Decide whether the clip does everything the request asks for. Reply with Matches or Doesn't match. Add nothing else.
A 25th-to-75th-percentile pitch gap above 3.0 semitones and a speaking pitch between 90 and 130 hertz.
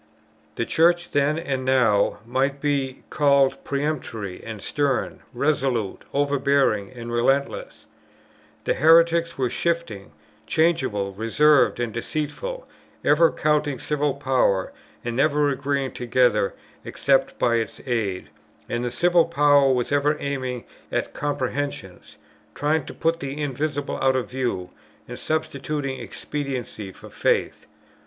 Doesn't match